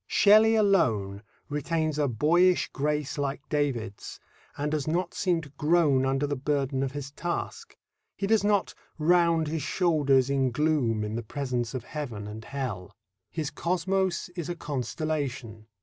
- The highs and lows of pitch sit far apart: No, average, 4.3 semitones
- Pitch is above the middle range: No, medium, 145 Hz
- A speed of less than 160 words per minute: Yes, average, 150 wpm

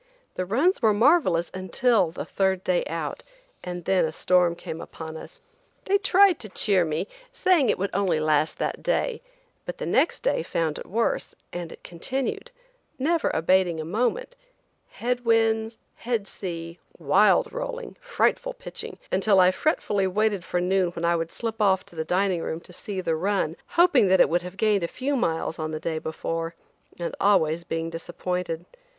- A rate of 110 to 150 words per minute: No, average, 180 wpm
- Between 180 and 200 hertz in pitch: Yes, medium, 185 Hz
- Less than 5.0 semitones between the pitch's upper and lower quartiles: No, average, 5.3 semitones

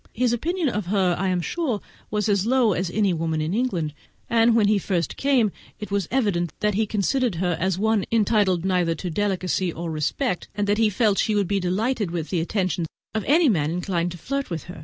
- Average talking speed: No, fast, 220 wpm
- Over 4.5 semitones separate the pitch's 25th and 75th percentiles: No, average, 4.1 semitones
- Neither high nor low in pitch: No, high, 200 Hz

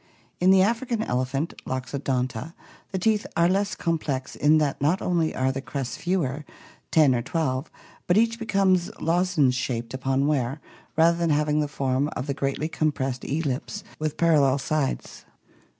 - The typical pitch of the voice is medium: Yes, medium, 150 Hz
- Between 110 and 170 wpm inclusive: Yes, average, 160 wpm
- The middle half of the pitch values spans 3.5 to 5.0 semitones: Yes, average, 4.5 semitones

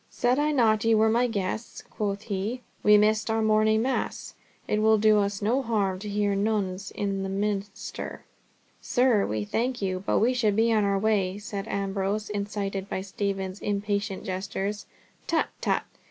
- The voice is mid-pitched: No, high, 210 Hz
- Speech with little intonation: Yes, narrow, 1.8 semitones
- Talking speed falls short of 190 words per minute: Yes, average, 170 wpm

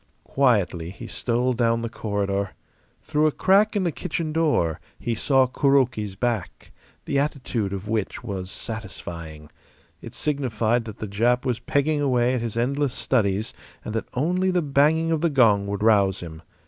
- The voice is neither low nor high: No, low, 120 Hz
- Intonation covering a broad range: Yes, wide, 5.7 semitones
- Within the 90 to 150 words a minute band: No, average, 165 wpm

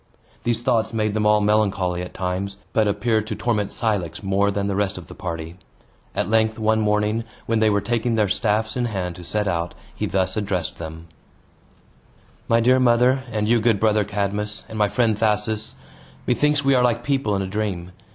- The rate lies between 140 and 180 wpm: No, average, 195 wpm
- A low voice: Yes, low, 105 Hz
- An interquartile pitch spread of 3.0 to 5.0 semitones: No, narrow, 2.4 semitones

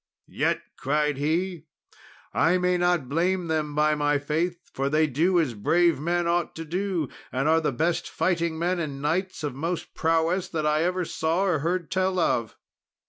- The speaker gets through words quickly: No, average, 180 wpm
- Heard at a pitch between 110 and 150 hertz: No, medium, 165 Hz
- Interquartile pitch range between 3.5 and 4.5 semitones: No, average, 2.8 semitones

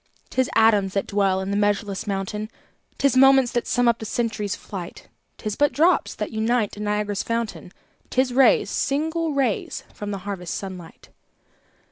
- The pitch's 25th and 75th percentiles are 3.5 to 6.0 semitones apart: Yes, average, 3.9 semitones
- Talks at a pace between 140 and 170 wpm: Yes, average, 165 wpm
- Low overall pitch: No, high, 215 Hz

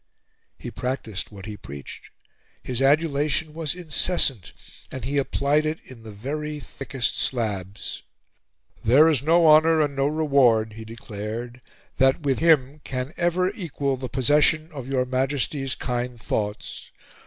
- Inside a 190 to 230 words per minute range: No, average, 140 wpm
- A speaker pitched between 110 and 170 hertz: Yes, low, 135 Hz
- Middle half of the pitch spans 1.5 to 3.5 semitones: No, average, 4.2 semitones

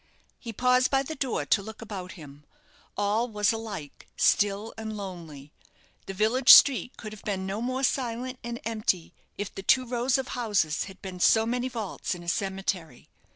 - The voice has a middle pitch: No, high, 215 Hz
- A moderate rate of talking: Yes, average, 180 wpm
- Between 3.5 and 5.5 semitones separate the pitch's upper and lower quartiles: Yes, average, 4.1 semitones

